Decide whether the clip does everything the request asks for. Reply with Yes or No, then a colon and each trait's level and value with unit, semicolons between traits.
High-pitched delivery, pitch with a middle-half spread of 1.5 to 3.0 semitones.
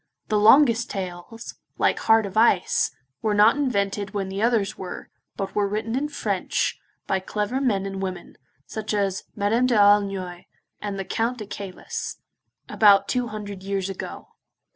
Yes: high, 205 Hz; narrow, 2.6 semitones